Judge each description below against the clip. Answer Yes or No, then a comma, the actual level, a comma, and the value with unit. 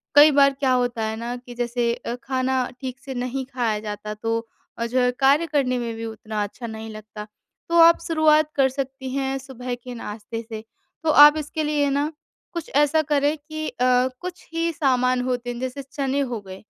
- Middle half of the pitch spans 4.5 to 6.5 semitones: No, average, 3.3 semitones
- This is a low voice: No, very high, 255 Hz